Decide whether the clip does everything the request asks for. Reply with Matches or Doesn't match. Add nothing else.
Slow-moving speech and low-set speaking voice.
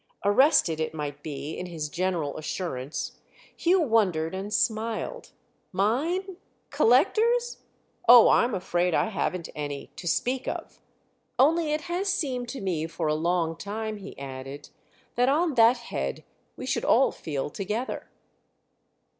Doesn't match